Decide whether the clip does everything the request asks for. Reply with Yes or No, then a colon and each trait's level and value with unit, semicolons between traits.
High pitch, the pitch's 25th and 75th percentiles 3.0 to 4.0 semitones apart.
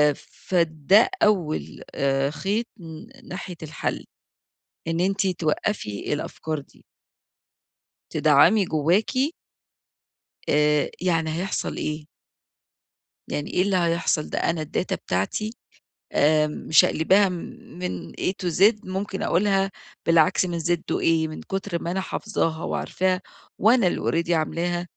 No: medium, 175 Hz; average, 3.7 semitones